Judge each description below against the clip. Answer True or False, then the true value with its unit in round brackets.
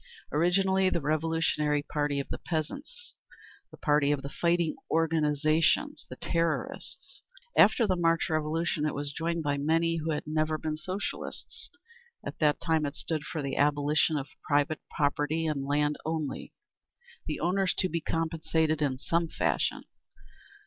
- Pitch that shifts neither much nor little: False (2.1 semitones)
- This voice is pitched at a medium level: True (155 Hz)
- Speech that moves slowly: False (145 wpm)